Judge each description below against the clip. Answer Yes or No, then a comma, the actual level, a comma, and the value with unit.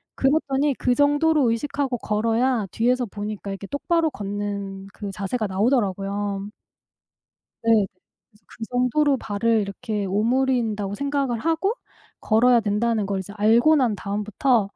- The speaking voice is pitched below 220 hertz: No, high, 225 Hz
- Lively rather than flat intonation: No, average, 4.5 semitones